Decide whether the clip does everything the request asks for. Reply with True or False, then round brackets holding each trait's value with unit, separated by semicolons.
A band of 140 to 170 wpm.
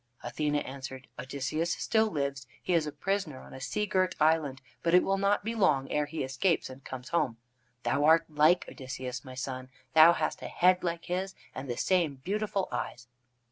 False (190 wpm)